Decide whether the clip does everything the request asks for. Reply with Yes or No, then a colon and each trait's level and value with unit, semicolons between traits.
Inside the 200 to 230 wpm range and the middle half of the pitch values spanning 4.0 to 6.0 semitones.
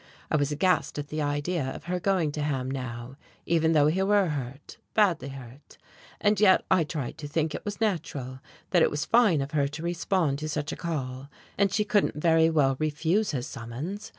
Yes: fast, 205 wpm; average, 4.6 semitones